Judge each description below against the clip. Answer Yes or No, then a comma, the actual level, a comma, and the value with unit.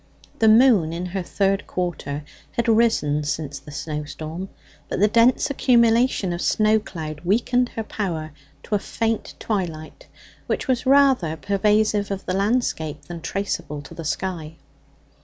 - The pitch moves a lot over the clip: Yes, wide, 6.0 semitones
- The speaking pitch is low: No, high, 195 Hz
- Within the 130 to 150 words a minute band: Yes, average, 145 wpm